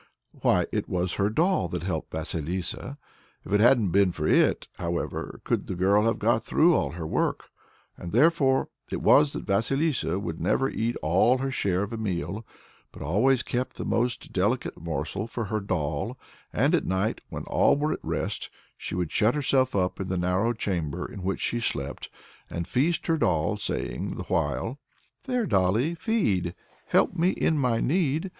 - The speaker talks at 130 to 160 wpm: No, average, 180 wpm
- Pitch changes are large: Yes, wide, 6.7 semitones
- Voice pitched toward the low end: Yes, low, 105 Hz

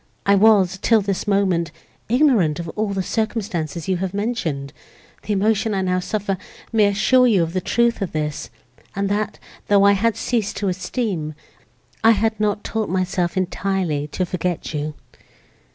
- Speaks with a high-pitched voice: Yes, high, 195 Hz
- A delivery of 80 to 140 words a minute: No, average, 165 wpm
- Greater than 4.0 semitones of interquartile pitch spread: No, average, 3.3 semitones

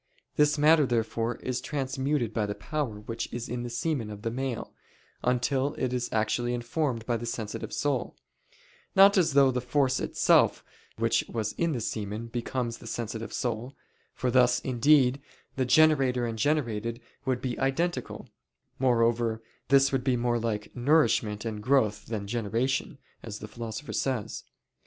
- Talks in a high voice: No, low, 125 Hz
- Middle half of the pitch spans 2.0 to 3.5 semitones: Yes, average, 2.9 semitones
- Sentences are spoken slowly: No, average, 155 wpm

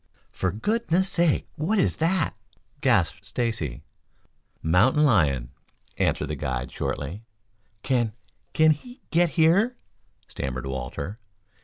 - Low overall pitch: Yes, low, 120 Hz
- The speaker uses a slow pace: Yes, slow, 110 wpm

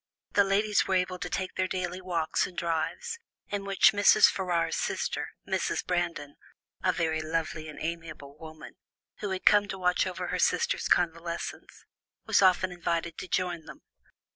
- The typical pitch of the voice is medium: Yes, medium, 180 Hz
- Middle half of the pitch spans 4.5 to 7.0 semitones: No, narrow, 2.4 semitones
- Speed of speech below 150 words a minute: No, average, 165 wpm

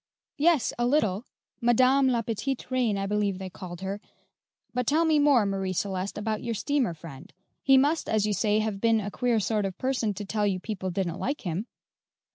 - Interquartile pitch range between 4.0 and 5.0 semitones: Yes, average, 4.5 semitones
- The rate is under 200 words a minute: No, fast, 205 wpm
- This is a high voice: Yes, high, 215 Hz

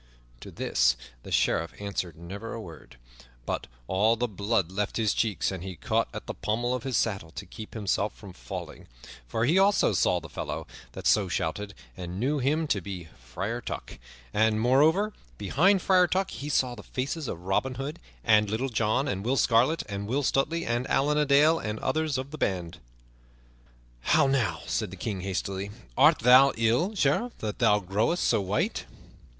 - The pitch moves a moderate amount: No, wide, 5.8 semitones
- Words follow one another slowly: No, average, 185 wpm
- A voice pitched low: Yes, low, 110 Hz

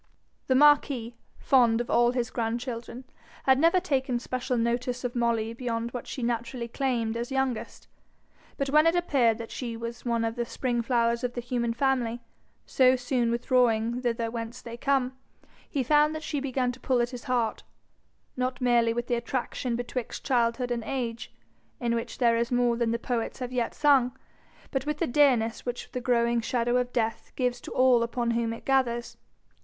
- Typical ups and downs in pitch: No, narrow, 1.7 semitones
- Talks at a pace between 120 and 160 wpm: No, average, 185 wpm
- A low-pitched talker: No, high, 245 Hz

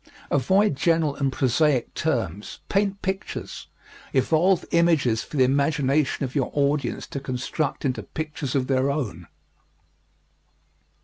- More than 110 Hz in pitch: Yes, medium, 140 Hz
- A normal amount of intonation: Yes, average, 3.4 semitones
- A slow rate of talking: Yes, slow, 120 wpm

